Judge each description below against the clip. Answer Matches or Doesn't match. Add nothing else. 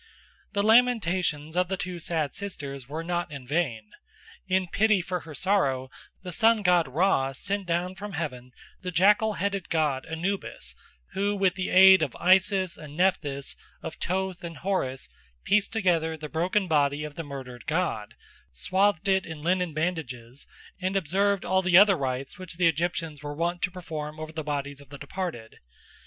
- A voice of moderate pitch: Matches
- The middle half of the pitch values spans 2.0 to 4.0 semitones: Doesn't match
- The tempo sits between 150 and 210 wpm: Matches